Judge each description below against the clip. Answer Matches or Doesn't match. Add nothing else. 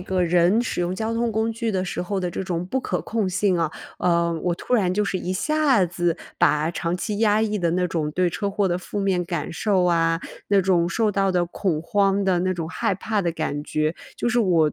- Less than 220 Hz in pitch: Matches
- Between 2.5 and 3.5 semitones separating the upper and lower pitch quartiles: Matches